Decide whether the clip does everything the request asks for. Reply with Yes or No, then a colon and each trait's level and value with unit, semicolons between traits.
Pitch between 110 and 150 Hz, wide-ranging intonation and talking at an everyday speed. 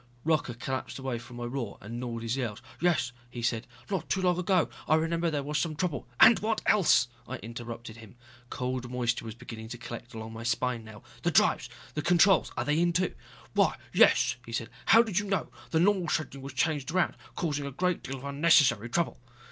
No: low, 135 Hz; wide, 6.1 semitones; fast, 210 wpm